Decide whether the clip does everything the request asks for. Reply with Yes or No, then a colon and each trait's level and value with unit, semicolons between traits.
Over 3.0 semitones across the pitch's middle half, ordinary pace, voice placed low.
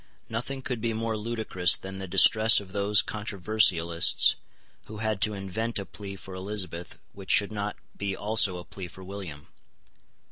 No: narrow, 2.4 semitones; average, 165 wpm; low, 100 Hz